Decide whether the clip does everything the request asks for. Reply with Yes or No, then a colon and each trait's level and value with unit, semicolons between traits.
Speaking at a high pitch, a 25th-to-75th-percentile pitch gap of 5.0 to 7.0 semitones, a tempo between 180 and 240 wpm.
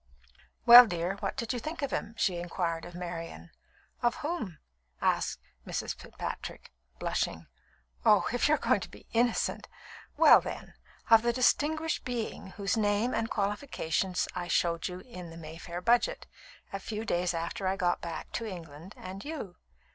No: high, 195 Hz; average, 5.3 semitones; average, 160 wpm